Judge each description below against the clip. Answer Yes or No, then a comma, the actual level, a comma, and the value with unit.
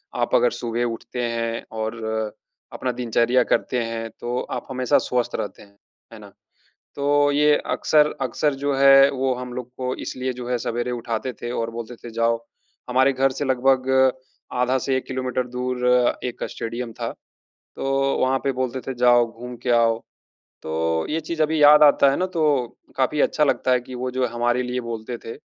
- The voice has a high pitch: No, low, 125 Hz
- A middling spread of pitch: No, narrow, 2.0 semitones